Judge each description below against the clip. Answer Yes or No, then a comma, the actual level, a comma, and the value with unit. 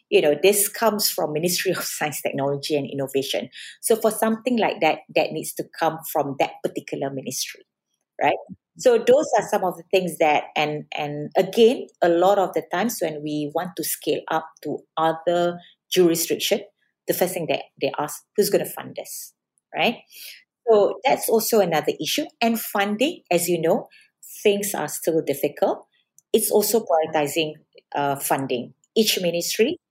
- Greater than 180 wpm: No, average, 165 wpm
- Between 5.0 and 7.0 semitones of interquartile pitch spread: Yes, wide, 5.5 semitones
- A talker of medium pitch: Yes, medium, 175 Hz